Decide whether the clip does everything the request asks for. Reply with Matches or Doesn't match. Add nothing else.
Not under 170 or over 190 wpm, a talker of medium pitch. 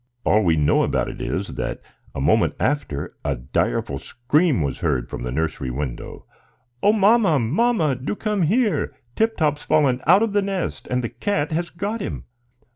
Matches